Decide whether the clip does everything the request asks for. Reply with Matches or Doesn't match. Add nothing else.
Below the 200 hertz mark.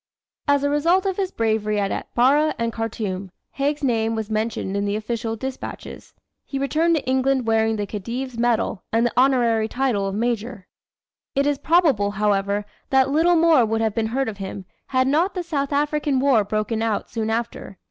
Doesn't match